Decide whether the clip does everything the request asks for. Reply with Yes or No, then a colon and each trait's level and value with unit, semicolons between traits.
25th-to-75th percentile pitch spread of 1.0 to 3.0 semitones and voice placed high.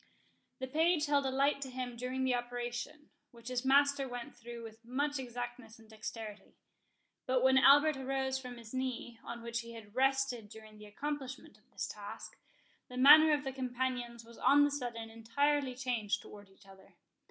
Yes: narrow, 2.6 semitones; very high, 250 Hz